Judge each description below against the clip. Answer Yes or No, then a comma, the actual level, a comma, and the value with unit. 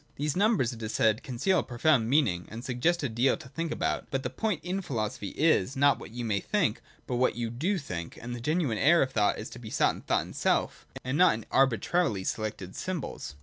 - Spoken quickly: Yes, fast, 230 wpm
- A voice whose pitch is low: Yes, low, 130 Hz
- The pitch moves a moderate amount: No, wide, 6.1 semitones